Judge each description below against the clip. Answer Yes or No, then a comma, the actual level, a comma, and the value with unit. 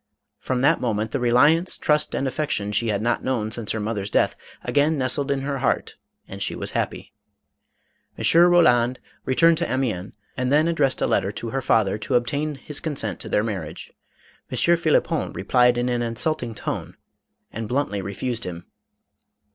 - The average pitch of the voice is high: No, low, 125 Hz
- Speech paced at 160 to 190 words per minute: Yes, average, 180 wpm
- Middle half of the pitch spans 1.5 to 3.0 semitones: No, average, 4.7 semitones